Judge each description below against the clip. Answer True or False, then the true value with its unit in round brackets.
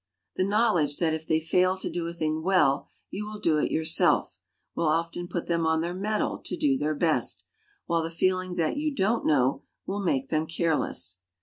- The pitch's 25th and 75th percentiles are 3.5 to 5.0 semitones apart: False (3.0 semitones)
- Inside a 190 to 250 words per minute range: True (200 wpm)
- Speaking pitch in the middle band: True (170 Hz)